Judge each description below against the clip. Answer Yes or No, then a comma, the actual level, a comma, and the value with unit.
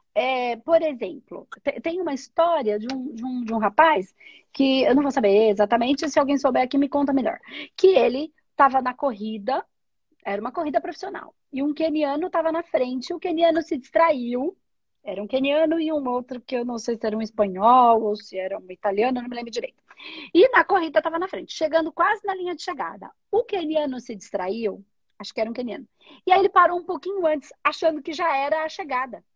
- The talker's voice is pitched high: Yes, very high, 285 Hz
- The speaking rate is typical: No, fast, 210 wpm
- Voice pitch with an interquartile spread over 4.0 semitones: Yes, average, 5.2 semitones